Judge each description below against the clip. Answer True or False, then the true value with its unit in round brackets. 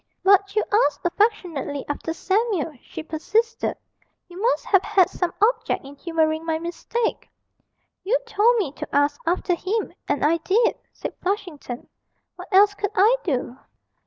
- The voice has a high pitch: True (370 Hz)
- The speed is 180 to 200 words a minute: False (150 wpm)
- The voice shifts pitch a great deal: False (4.9 semitones)